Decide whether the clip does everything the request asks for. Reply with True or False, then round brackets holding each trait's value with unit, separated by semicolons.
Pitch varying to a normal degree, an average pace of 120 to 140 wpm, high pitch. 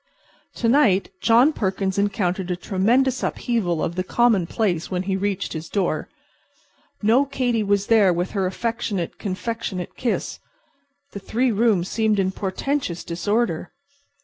True (4.0 semitones; 135 wpm; 200 Hz)